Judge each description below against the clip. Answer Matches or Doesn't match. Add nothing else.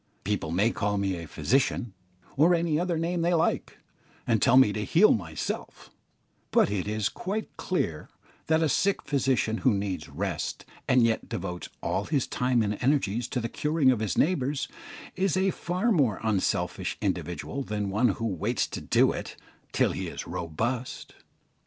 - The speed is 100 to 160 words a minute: Doesn't match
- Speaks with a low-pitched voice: Matches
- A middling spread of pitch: Doesn't match